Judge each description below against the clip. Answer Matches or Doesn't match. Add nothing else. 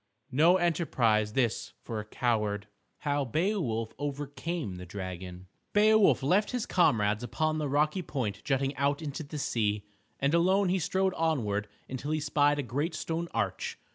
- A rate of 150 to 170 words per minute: Matches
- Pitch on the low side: Doesn't match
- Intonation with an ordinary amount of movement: Doesn't match